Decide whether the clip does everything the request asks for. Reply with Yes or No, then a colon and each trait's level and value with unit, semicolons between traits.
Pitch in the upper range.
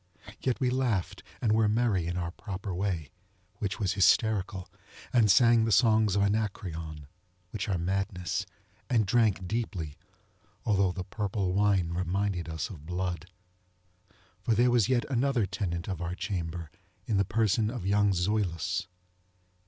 No: low, 100 Hz